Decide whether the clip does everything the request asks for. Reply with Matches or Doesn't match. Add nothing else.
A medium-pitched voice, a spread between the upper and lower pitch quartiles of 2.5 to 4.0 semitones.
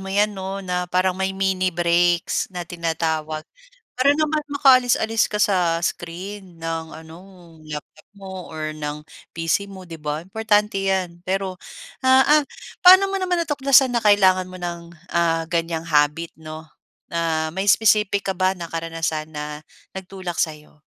Matches